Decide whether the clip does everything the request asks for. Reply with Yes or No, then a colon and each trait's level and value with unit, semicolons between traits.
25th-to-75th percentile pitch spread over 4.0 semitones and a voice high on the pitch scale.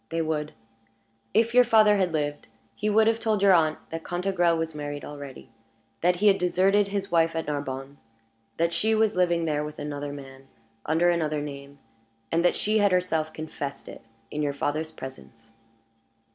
No: average, 4.8 semitones; medium, 165 Hz